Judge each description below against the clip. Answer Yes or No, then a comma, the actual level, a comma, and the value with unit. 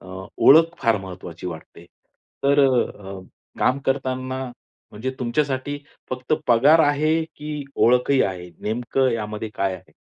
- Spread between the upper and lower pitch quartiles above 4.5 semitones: Yes, average, 5.3 semitones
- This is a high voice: No, low, 125 Hz